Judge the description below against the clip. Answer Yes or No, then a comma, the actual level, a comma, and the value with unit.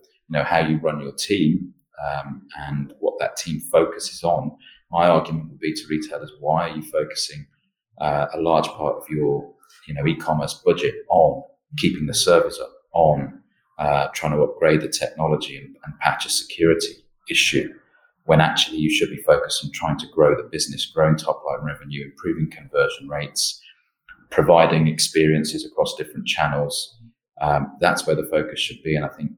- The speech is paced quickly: No, average, 175 wpm